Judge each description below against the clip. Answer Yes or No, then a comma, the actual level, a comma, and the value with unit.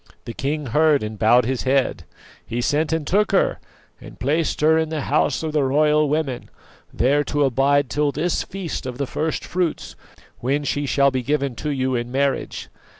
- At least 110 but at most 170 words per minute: No, average, 190 wpm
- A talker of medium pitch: Yes, medium, 145 Hz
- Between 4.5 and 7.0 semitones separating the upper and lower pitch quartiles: No, average, 2.8 semitones